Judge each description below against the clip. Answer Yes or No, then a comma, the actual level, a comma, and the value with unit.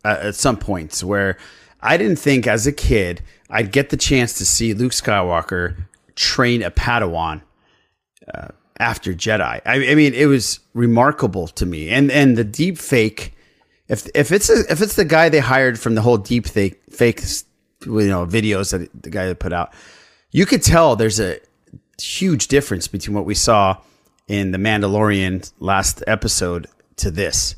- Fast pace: No, average, 175 wpm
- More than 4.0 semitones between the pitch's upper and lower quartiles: Yes, average, 5.3 semitones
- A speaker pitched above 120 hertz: No, low, 105 Hz